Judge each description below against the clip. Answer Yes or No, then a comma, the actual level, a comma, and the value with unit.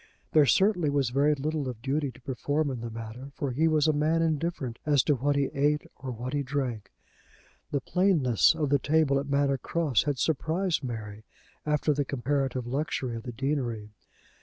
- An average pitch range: Yes, average, 3.2 semitones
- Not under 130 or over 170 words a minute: No, average, 185 wpm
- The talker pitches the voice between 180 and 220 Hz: No, medium, 140 Hz